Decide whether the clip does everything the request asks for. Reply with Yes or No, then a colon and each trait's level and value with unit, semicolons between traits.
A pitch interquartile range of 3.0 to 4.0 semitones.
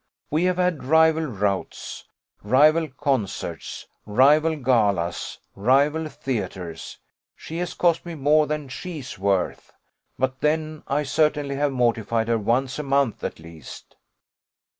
No: average, 5.2 semitones